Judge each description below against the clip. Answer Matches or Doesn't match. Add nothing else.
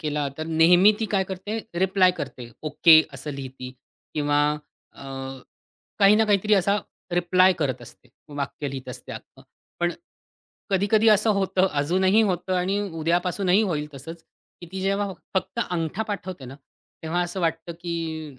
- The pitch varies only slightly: Doesn't match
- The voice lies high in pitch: Doesn't match